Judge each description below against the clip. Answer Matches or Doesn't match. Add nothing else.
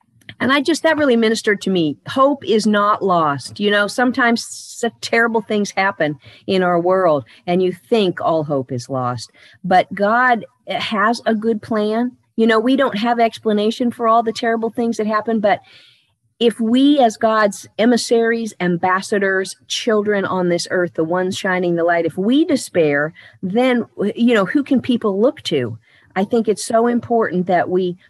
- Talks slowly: Doesn't match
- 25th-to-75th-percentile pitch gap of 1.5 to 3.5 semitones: Doesn't match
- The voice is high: Matches